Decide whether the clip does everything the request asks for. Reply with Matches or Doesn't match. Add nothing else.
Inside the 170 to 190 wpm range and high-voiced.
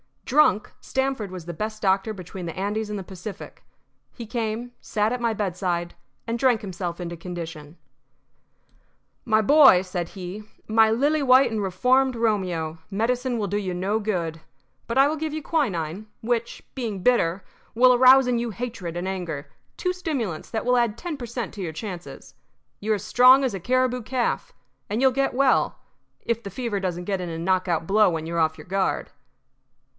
Matches